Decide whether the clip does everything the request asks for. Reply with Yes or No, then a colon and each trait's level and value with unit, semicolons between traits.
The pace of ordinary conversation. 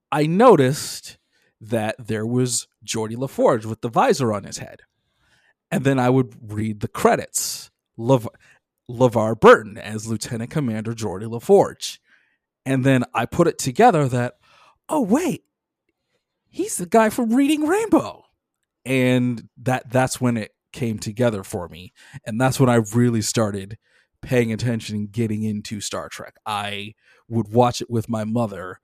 Yes: average, 150 wpm